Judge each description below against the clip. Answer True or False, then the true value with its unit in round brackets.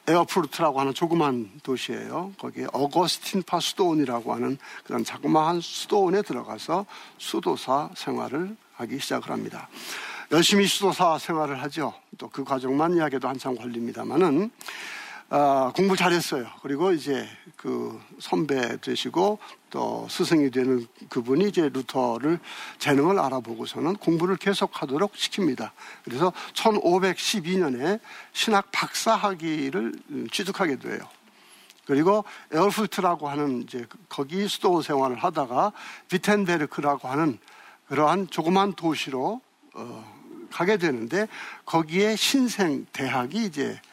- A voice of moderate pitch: True (165 Hz)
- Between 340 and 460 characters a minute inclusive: False (295 characters per minute)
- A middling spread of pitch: False (6.1 semitones)